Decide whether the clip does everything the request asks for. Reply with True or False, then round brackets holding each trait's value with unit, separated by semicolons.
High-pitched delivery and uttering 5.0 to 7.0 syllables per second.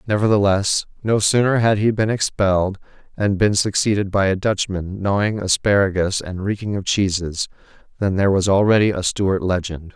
False (100 Hz; 5.1 syllables/s)